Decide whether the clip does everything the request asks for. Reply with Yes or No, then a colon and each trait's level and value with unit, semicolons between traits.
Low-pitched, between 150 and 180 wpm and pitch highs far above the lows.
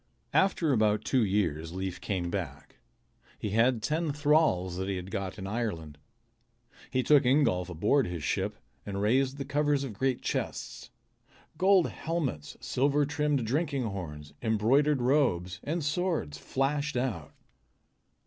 No: low, 120 Hz; average, 140 wpm; wide, 7.6 semitones